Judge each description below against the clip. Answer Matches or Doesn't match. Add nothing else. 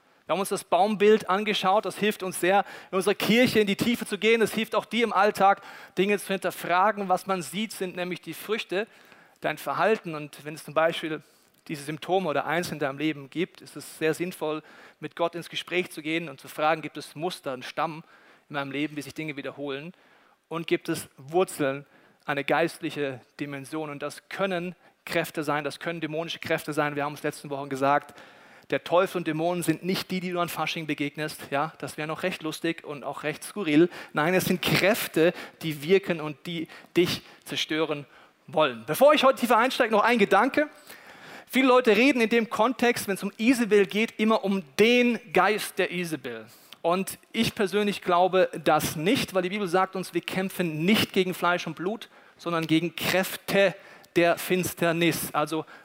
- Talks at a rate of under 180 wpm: Doesn't match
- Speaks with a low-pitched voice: Doesn't match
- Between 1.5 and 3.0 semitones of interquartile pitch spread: Doesn't match